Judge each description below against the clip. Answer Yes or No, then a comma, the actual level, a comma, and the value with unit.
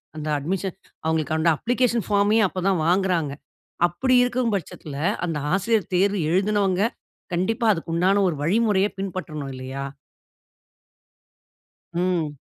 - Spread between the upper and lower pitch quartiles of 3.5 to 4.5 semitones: Yes, average, 4.0 semitones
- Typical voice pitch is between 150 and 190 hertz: Yes, medium, 185 Hz